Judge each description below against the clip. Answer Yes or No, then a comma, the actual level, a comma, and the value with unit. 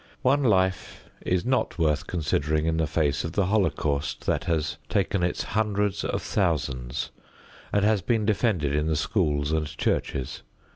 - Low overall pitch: Yes, very low, 85 Hz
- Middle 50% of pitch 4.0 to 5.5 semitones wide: Yes, average, 5.2 semitones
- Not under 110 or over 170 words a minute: Yes, average, 155 wpm